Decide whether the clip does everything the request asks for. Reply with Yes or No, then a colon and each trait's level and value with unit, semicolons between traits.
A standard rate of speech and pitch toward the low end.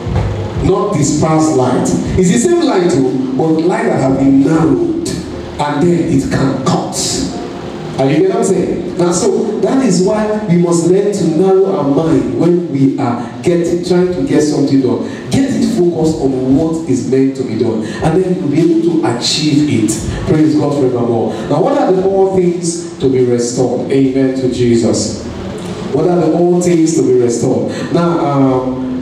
No: average, 190 wpm; medium, 155 Hz